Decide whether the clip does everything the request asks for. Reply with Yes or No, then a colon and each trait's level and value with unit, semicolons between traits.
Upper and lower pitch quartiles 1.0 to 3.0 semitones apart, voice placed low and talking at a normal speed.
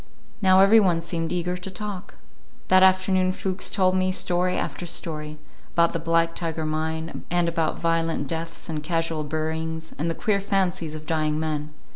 No: narrow, 2.5 semitones; medium, 165 Hz; average, 170 wpm